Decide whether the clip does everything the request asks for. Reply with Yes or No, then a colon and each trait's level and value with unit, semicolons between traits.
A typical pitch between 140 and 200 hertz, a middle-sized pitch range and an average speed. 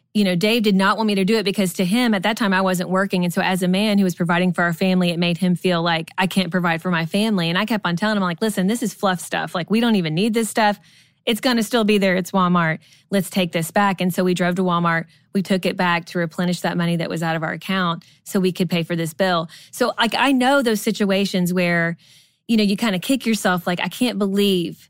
No: medium, 185 Hz; average, 3.1 semitones; fast, 280 wpm